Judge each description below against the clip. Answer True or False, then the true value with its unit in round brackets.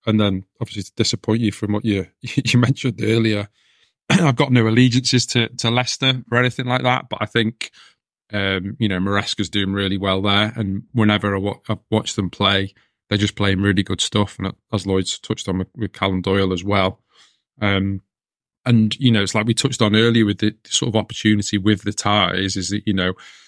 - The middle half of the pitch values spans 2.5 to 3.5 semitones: True (2.8 semitones)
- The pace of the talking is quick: True (210 wpm)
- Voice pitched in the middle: False (105 Hz)